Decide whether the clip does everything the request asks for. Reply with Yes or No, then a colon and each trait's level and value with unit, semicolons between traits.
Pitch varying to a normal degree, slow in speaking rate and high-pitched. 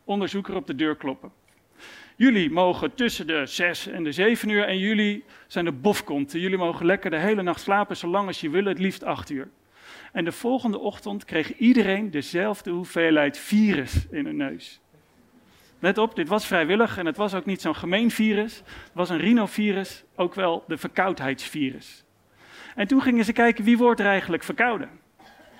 No: average, 4.0 semitones; average, 185 wpm; high, 195 Hz